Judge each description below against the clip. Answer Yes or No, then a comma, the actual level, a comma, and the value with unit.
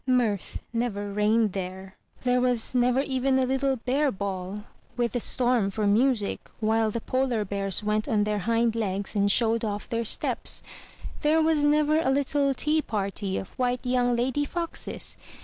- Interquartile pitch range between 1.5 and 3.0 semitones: No, average, 4.1 semitones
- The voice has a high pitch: Yes, high, 230 Hz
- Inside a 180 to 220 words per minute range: No, average, 165 wpm